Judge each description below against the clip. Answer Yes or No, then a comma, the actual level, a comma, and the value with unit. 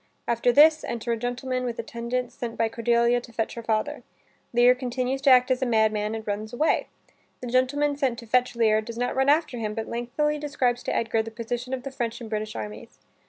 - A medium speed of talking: No, fast, 215 wpm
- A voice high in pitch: Yes, high, 240 Hz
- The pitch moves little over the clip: Yes, narrow, 2.0 semitones